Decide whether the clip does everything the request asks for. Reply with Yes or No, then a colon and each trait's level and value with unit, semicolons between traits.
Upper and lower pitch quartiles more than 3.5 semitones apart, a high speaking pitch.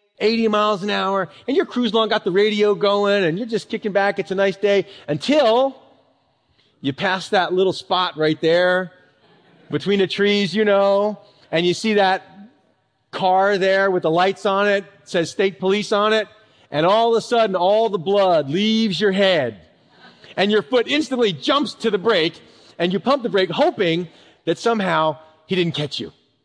No: average, 2.9 semitones; high, 200 Hz